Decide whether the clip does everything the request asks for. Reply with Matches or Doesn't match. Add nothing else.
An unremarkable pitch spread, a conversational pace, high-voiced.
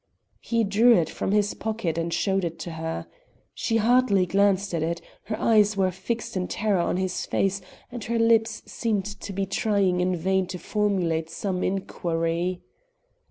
Matches